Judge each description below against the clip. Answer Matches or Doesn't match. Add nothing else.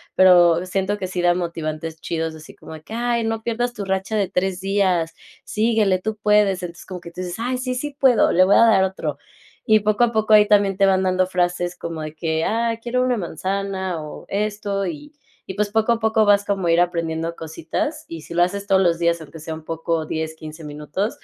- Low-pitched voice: Doesn't match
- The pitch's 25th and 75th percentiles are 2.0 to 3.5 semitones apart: Doesn't match